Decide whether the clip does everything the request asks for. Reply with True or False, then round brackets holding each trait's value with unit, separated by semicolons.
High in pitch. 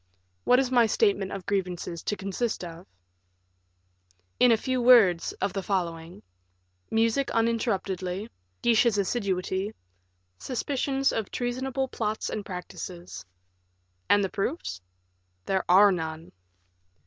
True (205 Hz)